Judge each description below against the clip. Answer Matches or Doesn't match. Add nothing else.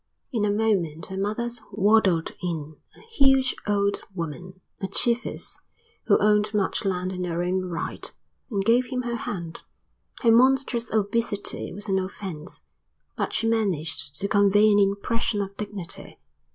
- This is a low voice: Doesn't match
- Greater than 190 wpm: Doesn't match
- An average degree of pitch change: Matches